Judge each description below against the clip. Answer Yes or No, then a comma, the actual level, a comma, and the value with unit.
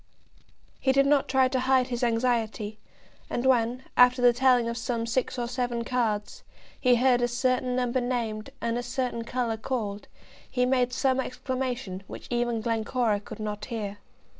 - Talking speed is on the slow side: No, average, 165 wpm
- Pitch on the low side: No, high, 245 Hz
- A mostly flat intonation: Yes, narrow, 1.8 semitones